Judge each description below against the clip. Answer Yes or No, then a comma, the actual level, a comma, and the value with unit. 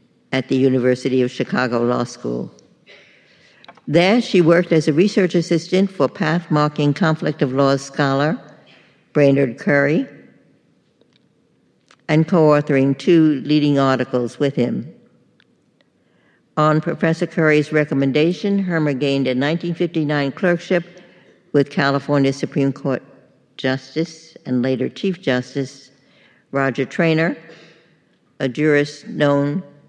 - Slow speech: Yes, slow, 105 wpm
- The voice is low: No, medium, 150 Hz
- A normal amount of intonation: Yes, average, 3.3 semitones